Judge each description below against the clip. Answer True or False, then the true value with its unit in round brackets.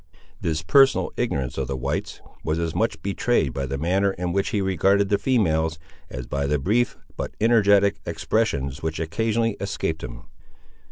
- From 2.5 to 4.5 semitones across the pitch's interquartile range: False (5.0 semitones)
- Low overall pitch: True (85 Hz)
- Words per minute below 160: False (165 wpm)